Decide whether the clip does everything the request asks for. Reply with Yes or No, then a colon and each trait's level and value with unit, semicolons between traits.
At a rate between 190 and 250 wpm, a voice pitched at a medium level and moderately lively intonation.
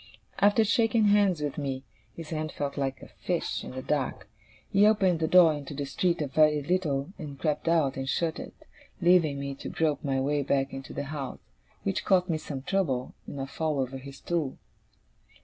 Yes: average, 200 wpm; medium, 150 Hz; average, 3.9 semitones